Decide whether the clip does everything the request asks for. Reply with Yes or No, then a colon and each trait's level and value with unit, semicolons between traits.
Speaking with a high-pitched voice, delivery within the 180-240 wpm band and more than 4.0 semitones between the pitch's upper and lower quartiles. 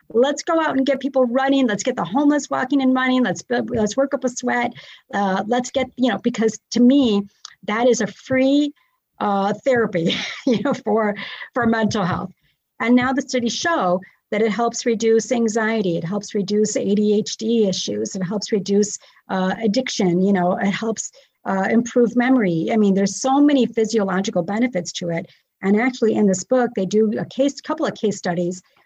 Yes: high, 225 Hz; average, 185 wpm; average, 4.4 semitones